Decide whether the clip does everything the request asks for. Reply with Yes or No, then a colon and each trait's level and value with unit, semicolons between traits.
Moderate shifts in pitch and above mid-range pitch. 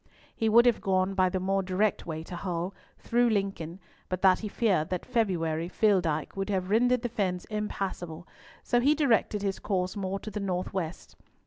Yes: average, 3.0 semitones; high, 195 Hz